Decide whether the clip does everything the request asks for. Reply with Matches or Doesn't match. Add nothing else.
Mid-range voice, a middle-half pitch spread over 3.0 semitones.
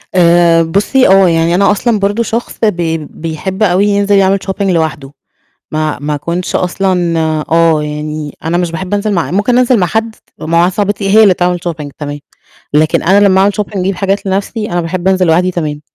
Matches